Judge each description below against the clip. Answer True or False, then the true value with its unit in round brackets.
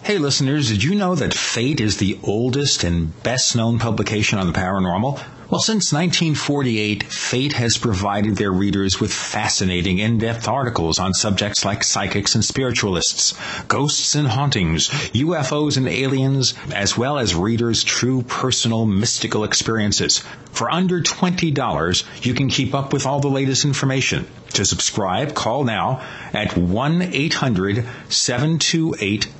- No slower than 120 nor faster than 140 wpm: True (135 wpm)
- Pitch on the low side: True (120 Hz)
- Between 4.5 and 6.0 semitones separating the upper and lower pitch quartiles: True (5.3 semitones)